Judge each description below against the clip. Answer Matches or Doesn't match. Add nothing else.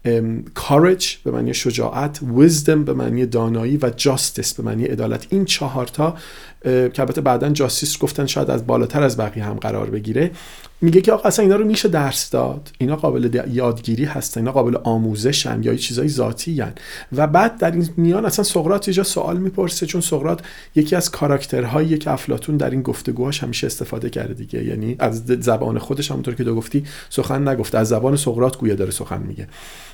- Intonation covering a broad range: Doesn't match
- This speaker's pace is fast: Matches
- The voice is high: Doesn't match